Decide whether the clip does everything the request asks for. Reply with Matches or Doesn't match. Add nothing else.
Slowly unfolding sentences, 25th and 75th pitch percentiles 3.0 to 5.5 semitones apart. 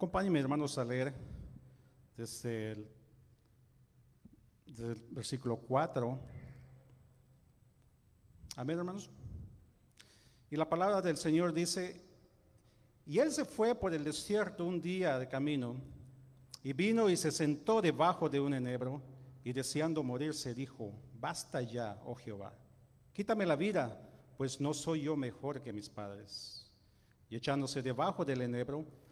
Matches